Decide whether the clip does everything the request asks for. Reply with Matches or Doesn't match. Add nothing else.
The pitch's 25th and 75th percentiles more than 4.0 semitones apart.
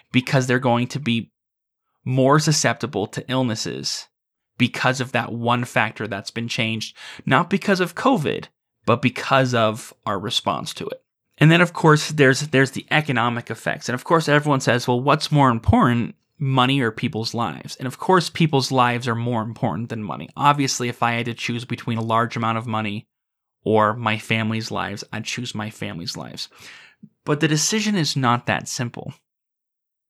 Doesn't match